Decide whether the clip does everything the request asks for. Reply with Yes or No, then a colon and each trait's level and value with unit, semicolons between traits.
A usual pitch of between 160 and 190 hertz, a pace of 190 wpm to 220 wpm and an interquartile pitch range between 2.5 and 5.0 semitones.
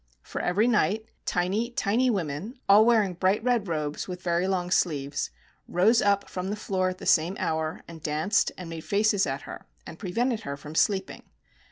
Yes: medium, 185 Hz; average, 200 wpm; average, 4.3 semitones